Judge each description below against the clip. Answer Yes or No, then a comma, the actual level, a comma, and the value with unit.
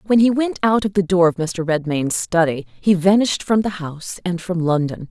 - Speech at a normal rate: No, fast, 225 wpm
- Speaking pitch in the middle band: Yes, medium, 180 Hz